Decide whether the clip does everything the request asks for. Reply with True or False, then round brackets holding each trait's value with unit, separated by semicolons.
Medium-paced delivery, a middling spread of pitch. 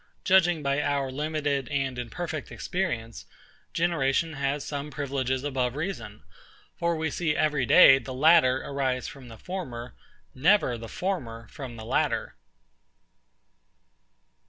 False (125 wpm; 3.8 semitones)